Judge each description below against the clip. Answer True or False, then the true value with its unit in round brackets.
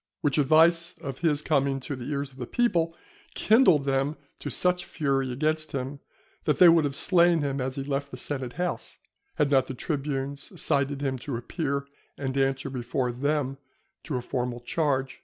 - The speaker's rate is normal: True (180 wpm)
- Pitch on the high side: False (140 Hz)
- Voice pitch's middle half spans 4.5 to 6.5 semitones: False (2.7 semitones)